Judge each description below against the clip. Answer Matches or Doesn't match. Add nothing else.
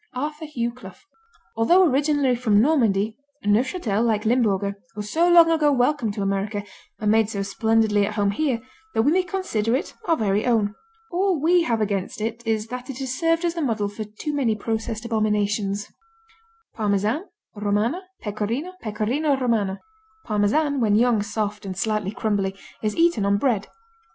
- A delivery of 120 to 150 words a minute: Doesn't match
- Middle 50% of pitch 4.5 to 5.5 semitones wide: Matches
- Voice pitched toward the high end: Matches